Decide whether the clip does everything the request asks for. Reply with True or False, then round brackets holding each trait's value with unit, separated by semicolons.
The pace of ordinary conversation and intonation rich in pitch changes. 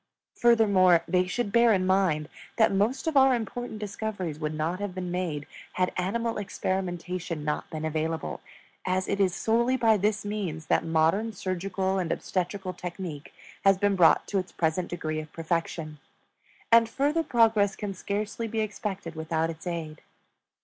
False (160 wpm; 4.3 semitones)